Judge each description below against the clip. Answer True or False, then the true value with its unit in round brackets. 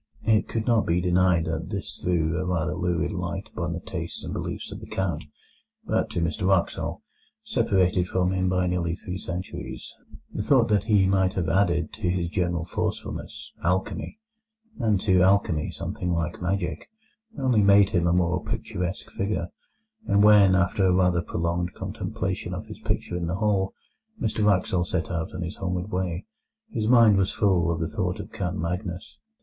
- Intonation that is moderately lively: False (2.3 semitones)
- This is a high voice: False (90 Hz)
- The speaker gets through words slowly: False (175 wpm)